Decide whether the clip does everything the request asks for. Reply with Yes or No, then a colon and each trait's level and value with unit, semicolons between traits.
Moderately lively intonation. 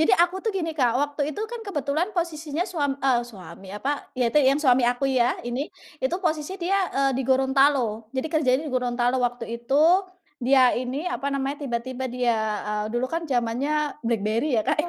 Yes: average, 3.6 semitones